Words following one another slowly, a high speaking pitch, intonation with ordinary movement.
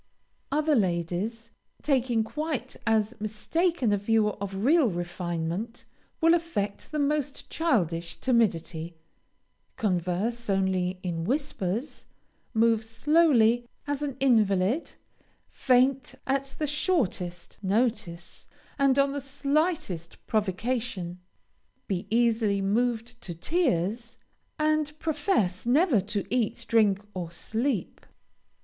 No: slow, 105 wpm; high, 230 Hz; wide, 6.4 semitones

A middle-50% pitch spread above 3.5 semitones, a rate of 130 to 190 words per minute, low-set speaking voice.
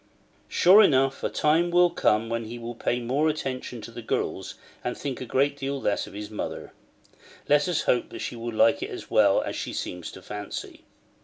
No: average, 4.1 semitones; fast, 205 wpm; low, 125 Hz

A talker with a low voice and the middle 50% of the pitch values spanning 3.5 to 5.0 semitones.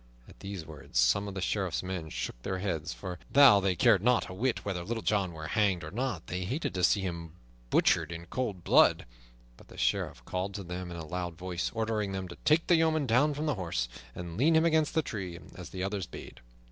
Yes: very low, 95 Hz; average, 4.6 semitones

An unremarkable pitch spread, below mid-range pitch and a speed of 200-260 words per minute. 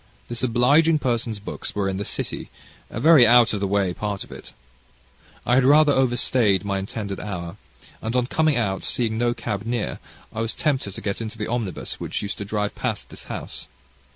Yes: average, 3.3 semitones; low, 115 Hz; fast, 205 wpm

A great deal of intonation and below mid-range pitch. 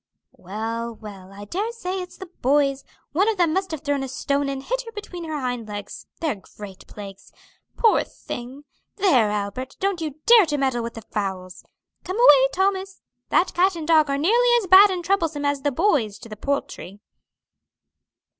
No: wide, 8.4 semitones; very high, 285 Hz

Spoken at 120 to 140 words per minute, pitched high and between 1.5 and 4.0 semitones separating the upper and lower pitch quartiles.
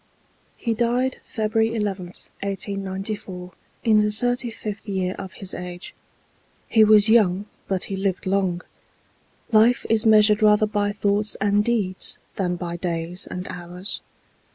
Yes: slow, 135 wpm; high, 205 Hz; average, 2.7 semitones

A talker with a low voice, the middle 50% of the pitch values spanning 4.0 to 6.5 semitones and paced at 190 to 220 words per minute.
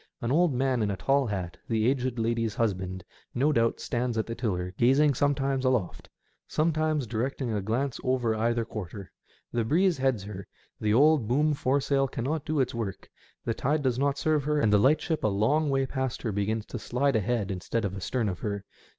Yes: low, 120 Hz; average, 4.3 semitones; average, 195 wpm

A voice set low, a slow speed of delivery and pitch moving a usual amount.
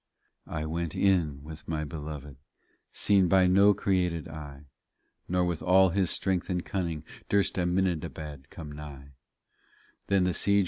Yes: very low, 85 Hz; slow, 130 wpm; average, 3.5 semitones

